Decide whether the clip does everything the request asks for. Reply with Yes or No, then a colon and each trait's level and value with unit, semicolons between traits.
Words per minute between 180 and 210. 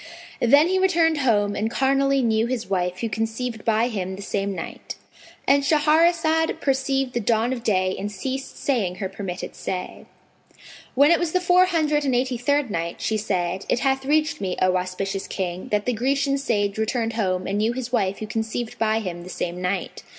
Yes: average, 190 wpm